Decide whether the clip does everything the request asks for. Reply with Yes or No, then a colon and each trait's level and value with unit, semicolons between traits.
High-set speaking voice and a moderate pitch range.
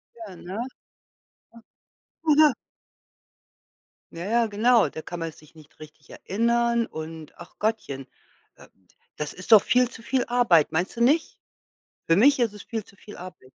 No: high, 210 Hz; wide, 6.3 semitones